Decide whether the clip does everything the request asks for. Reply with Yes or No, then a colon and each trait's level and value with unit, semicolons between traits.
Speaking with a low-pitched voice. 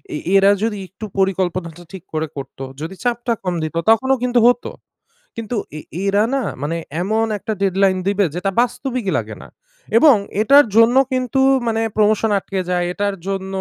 No: high, 205 Hz